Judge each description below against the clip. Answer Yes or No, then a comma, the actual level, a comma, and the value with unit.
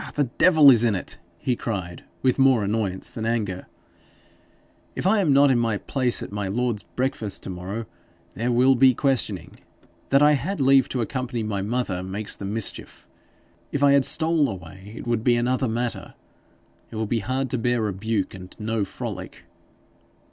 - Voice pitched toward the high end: No, low, 120 Hz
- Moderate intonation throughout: Yes, average, 4.5 semitones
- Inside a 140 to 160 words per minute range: No, average, 175 wpm